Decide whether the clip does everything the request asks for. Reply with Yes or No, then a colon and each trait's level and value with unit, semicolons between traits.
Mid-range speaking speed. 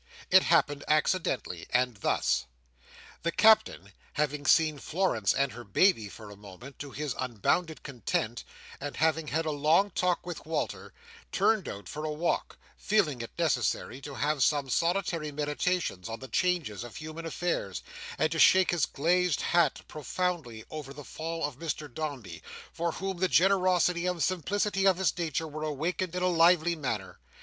Yes: average, 165 wpm